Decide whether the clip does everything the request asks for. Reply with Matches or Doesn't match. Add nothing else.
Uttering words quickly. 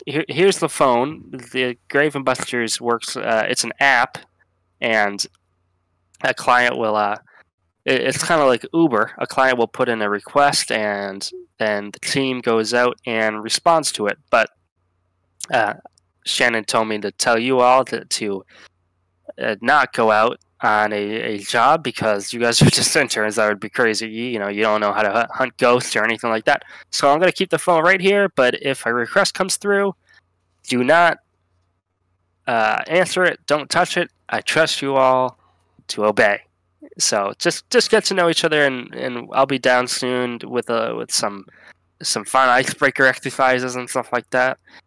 Doesn't match